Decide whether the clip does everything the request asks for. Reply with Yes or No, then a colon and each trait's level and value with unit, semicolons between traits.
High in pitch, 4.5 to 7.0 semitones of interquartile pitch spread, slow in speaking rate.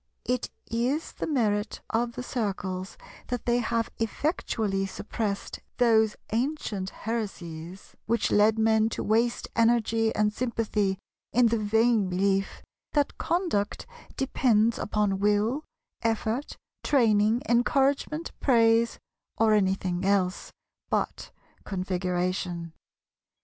No: high, 220 Hz; average, 3.1 semitones; slow, 105 wpm